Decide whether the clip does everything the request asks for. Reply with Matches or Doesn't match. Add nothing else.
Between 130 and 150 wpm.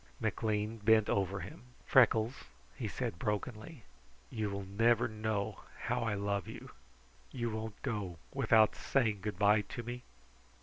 Matches